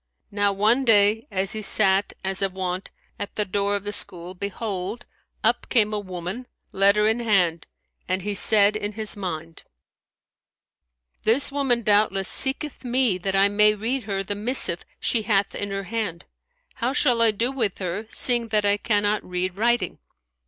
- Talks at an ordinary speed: Yes, average, 165 wpm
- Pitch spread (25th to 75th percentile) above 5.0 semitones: No, average, 2.7 semitones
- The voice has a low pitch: No, high, 205 Hz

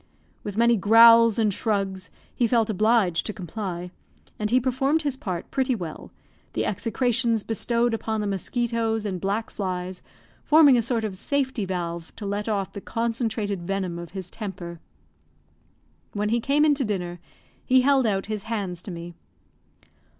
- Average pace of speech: Yes, average, 160 wpm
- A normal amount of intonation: Yes, average, 3.7 semitones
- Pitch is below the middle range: No, high, 215 Hz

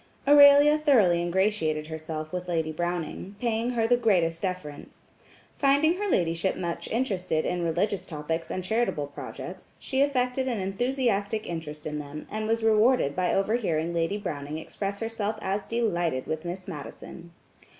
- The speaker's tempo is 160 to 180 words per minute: No, average, 150 wpm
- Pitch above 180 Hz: Yes, high, 190 Hz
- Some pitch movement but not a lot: No, wide, 5.7 semitones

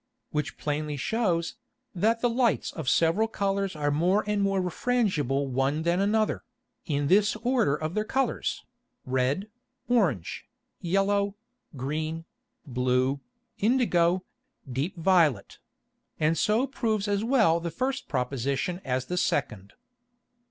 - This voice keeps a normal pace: No, slow, 125 wpm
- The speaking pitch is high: No, medium, 175 Hz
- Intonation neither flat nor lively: No, wide, 6.7 semitones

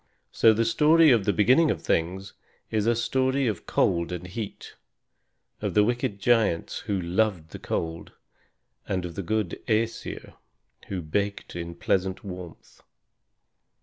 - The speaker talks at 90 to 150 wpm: Yes, average, 145 wpm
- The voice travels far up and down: No, average, 4.3 semitones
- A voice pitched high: No, low, 100 Hz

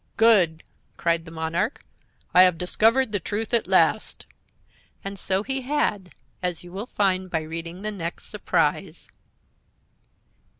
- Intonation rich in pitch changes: No, average, 4.2 semitones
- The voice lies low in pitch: No, medium, 185 Hz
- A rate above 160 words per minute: No, slow, 135 wpm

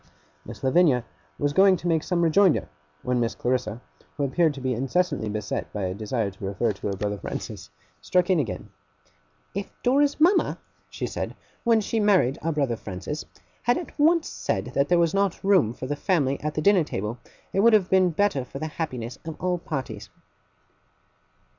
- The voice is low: No, medium, 150 Hz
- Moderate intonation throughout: No, wide, 7.6 semitones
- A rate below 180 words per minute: No, average, 190 wpm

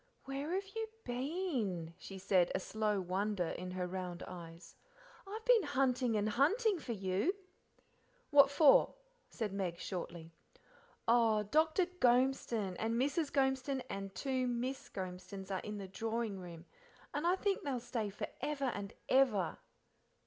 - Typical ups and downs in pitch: No, wide, 6.4 semitones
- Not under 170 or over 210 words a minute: No, average, 145 wpm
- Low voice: No, high, 230 Hz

